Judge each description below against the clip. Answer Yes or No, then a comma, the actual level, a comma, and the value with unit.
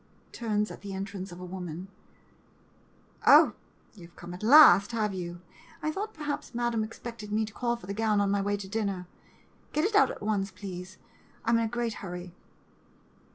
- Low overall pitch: No, high, 205 Hz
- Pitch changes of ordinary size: Yes, average, 3.6 semitones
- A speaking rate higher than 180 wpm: Yes, average, 190 wpm